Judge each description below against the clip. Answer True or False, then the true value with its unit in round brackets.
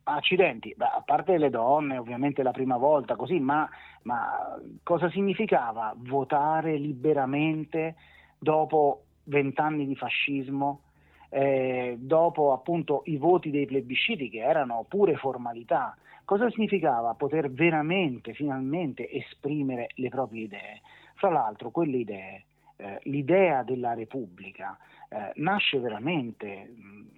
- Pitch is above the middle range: False (140 Hz)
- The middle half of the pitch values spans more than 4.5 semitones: False (3.6 semitones)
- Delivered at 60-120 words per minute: True (115 wpm)